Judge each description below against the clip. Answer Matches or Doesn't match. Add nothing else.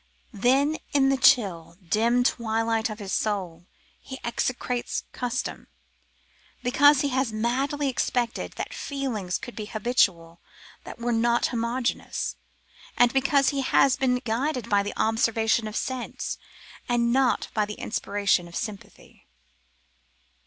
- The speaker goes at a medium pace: Doesn't match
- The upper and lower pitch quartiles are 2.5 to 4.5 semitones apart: Matches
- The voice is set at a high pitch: Matches